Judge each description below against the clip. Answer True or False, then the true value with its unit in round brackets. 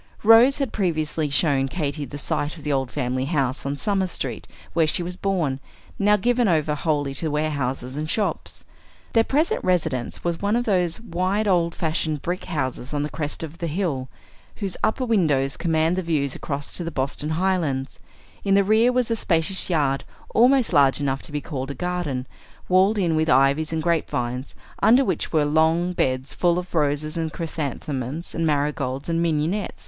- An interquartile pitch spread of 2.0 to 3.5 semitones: False (4.5 semitones)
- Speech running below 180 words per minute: False (185 wpm)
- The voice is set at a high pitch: False (160 Hz)